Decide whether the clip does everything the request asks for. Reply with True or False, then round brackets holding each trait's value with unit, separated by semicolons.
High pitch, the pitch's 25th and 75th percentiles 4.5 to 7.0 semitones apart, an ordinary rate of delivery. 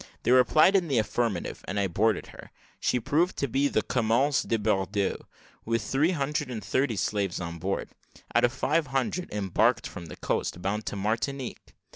False (115 Hz; 5.4 semitones; 180 wpm)